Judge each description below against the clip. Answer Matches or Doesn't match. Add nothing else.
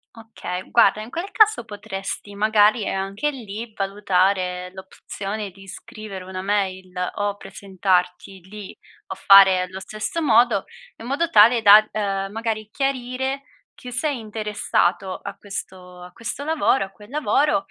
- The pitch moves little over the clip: Doesn't match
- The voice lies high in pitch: Matches